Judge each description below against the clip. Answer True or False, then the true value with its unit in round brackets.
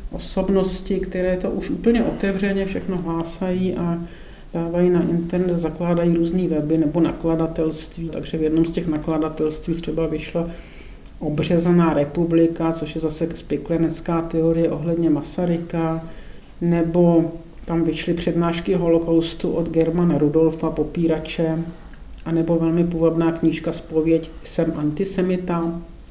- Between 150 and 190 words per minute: False (115 wpm)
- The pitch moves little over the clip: True (1.0 semitones)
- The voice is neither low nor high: True (165 Hz)